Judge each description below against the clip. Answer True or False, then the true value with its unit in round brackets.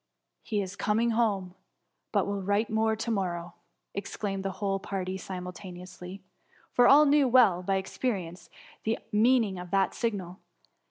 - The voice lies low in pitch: False (195 Hz)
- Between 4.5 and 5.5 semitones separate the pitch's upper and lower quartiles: False (3.2 semitones)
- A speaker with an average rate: True (155 wpm)